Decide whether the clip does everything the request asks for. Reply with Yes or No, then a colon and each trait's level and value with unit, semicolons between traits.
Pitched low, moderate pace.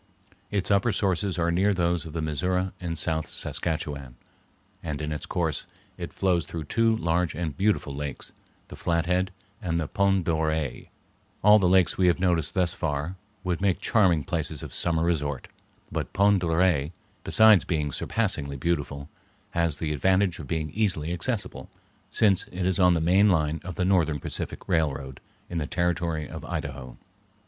Yes: very low, 85 Hz; average, 165 wpm